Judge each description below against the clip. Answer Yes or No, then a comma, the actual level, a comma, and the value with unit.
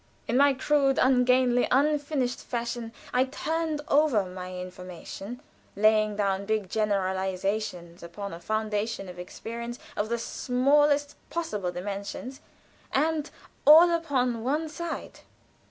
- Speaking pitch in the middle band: No, high, 235 Hz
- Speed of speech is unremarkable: No, slow, 115 wpm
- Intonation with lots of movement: Yes, wide, 6.1 semitones